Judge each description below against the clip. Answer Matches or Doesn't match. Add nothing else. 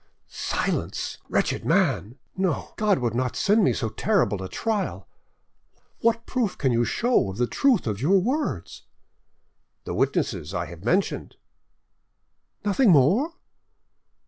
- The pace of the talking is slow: Matches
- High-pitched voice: Doesn't match